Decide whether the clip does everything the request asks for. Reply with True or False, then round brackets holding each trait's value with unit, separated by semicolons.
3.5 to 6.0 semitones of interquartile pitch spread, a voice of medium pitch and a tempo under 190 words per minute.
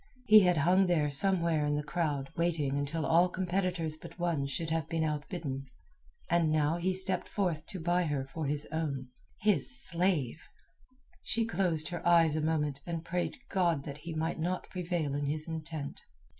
False (3.0 semitones; 165 Hz; 170 wpm)